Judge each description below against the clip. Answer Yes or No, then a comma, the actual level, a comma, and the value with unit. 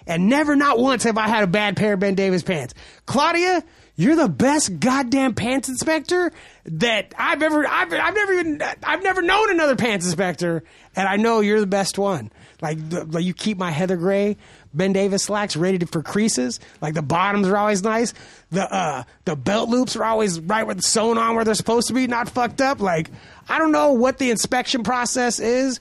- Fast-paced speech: Yes, fast, 210 wpm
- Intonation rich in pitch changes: Yes, wide, 5.9 semitones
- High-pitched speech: Yes, high, 220 Hz